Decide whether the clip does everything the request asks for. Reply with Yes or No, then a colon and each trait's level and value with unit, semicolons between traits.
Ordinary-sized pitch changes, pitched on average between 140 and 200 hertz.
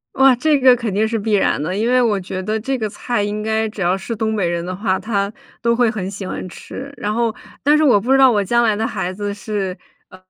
No: average, 3.2 semitones; high, 215 Hz